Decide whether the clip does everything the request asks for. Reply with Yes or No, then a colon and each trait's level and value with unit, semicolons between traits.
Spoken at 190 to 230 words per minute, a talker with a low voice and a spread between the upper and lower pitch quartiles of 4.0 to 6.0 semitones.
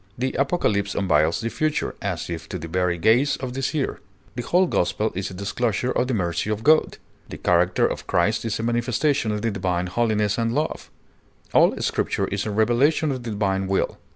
Yes: average, 200 wpm; low, 110 Hz; average, 4.7 semitones